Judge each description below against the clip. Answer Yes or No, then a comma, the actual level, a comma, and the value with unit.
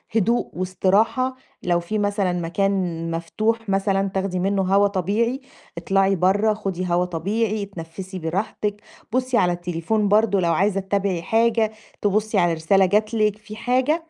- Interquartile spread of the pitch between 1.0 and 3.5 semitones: Yes, average, 3.0 semitones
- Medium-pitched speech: No, high, 195 Hz